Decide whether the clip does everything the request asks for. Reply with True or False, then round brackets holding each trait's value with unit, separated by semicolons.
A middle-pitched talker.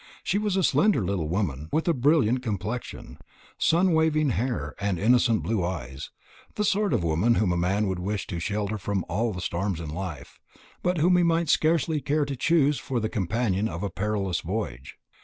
False (110 Hz)